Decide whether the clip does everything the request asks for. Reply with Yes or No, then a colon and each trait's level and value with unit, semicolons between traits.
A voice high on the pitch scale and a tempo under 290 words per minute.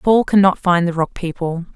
No: medium, 180 Hz; fast, 205 wpm